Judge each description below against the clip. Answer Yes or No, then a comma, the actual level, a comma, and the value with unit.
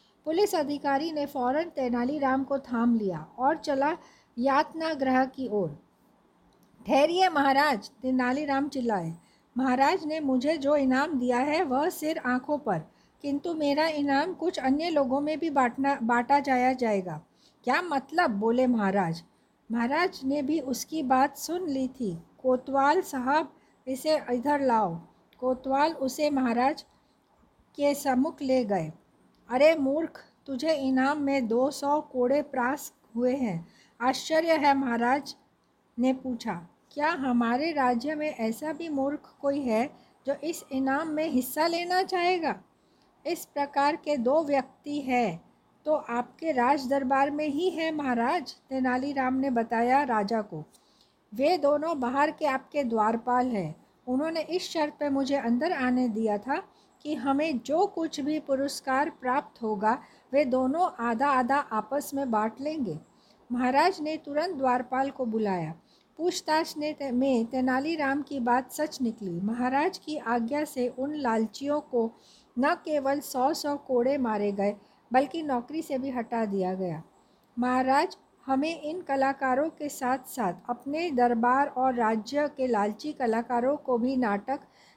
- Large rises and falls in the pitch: No, average, 3.3 semitones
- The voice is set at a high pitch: Yes, very high, 270 Hz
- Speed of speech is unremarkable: Yes, average, 140 wpm